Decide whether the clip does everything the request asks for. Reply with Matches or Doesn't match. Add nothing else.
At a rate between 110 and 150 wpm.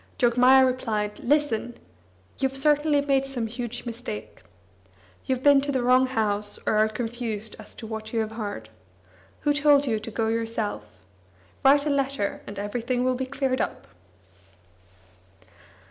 Matches